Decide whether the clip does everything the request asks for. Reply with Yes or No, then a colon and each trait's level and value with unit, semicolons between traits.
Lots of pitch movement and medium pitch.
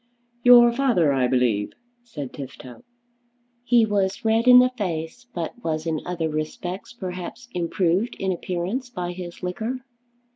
Yes: wide, 6.6 semitones; medium, 180 Hz